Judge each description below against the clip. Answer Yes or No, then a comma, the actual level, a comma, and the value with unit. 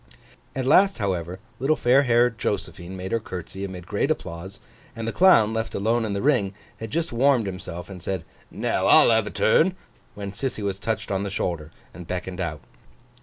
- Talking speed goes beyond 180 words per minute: Yes, average, 190 wpm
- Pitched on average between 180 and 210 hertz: No, low, 100 Hz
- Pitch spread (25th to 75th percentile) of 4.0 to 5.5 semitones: Yes, average, 4.3 semitones